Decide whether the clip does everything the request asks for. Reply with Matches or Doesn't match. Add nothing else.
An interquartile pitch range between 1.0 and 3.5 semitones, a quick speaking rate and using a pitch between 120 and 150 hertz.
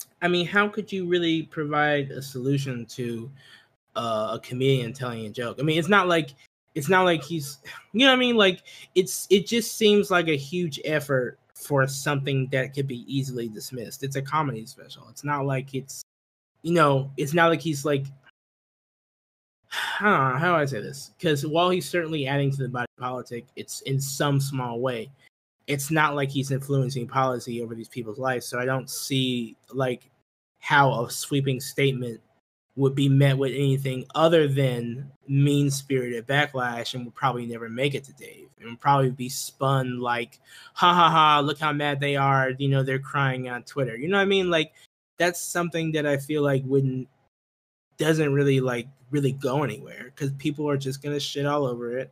Doesn't match